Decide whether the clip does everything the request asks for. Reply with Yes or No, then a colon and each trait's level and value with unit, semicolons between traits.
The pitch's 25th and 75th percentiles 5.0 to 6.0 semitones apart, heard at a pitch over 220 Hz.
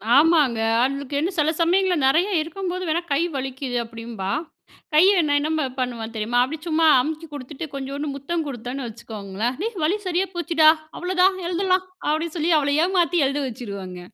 Yes: wide, 5.4 semitones; very high, 295 Hz